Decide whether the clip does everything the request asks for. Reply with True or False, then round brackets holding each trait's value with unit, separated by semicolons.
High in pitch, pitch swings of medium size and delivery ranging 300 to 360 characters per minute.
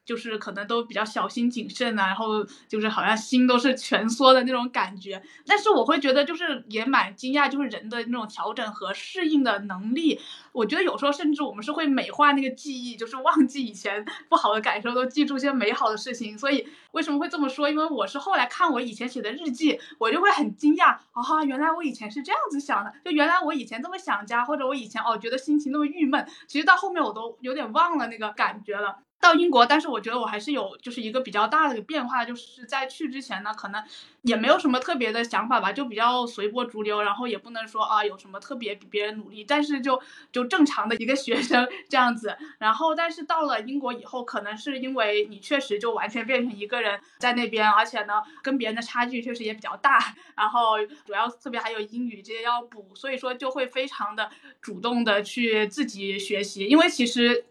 True (245 Hz; 4.5 semitones; 345 characters per minute)